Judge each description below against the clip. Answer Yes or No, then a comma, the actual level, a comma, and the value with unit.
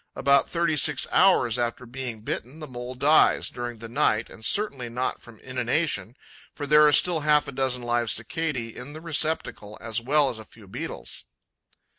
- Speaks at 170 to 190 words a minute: Yes, average, 180 wpm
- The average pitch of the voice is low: Yes, low, 130 Hz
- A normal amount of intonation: Yes, average, 4.3 semitones